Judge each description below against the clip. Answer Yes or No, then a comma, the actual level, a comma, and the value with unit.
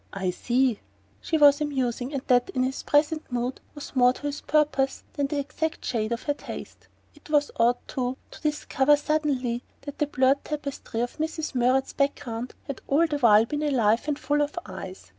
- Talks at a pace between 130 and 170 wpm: No, average, 190 wpm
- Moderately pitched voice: No, very high, 275 Hz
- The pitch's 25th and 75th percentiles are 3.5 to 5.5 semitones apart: No, average, 3.1 semitones